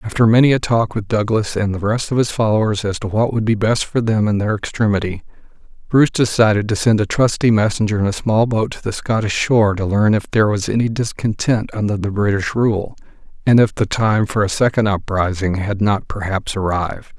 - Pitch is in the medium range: No, low, 105 Hz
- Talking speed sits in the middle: No, fast, 215 wpm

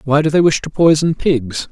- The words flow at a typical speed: No, fast, 245 wpm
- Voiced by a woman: No, male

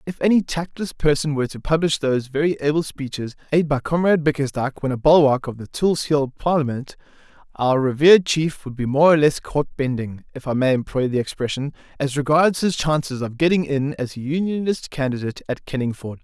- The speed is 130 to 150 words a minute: No, average, 190 wpm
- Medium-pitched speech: Yes, medium, 145 Hz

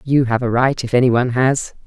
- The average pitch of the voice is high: No, low, 125 Hz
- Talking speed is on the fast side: Yes, fast, 260 wpm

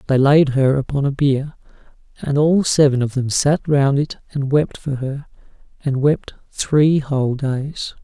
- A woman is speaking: No, male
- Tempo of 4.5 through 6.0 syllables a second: No, 4.1 syllables/s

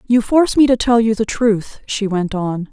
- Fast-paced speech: Yes, fast, 245 wpm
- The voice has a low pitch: No, high, 220 Hz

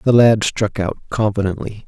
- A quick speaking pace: No, average, 160 wpm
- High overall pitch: No, low, 105 Hz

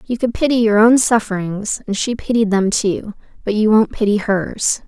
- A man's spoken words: No, female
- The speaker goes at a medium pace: Yes, average, 195 wpm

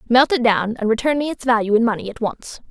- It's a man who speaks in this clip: No, female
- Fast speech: Yes, fast, 265 wpm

